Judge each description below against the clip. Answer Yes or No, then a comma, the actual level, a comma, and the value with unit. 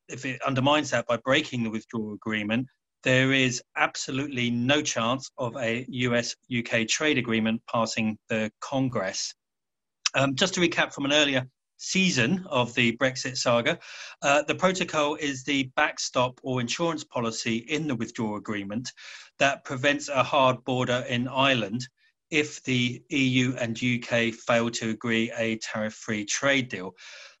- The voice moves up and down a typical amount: Yes, average, 3.7 semitones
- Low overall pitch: Yes, low, 125 Hz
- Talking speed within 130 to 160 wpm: Yes, average, 150 wpm